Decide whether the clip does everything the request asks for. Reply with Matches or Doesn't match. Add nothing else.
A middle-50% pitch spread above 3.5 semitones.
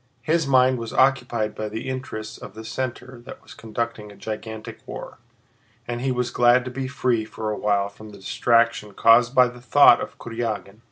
Doesn't match